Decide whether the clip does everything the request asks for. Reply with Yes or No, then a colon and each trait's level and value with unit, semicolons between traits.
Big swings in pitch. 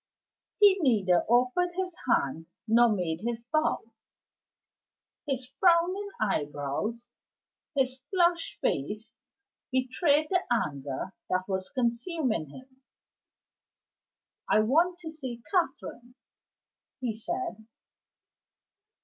Yes: wide, 7.6 semitones